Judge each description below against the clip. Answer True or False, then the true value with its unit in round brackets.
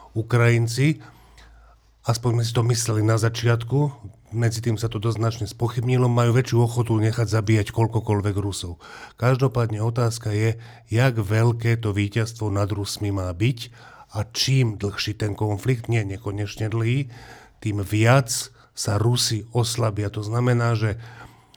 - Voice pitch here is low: True (115 Hz)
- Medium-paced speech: True (130 wpm)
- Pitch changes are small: True (2.0 semitones)